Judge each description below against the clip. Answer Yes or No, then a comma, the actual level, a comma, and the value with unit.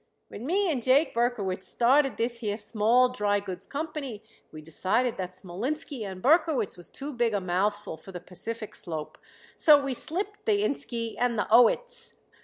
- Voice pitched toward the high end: Yes, high, 235 Hz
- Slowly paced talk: No, average, 165 wpm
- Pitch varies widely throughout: Yes, wide, 5.9 semitones